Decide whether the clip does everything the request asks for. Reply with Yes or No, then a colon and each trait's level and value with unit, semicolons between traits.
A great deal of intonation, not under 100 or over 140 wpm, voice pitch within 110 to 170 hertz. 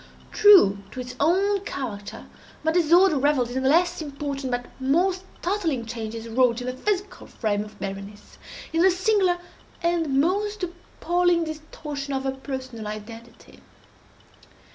No: wide, 6.7 semitones; slow, 135 wpm; very high, 280 Hz